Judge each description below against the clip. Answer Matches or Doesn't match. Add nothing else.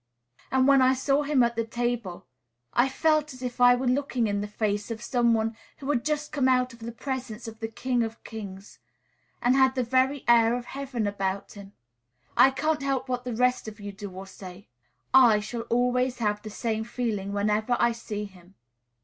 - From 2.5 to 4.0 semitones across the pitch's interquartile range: Matches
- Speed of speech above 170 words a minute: Matches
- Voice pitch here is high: Matches